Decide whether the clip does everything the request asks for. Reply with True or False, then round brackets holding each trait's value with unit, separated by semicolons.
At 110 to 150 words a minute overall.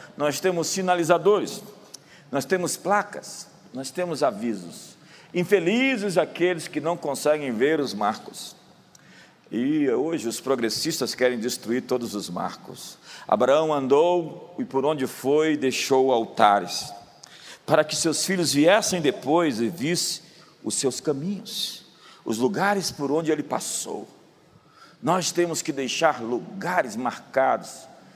True (120 wpm)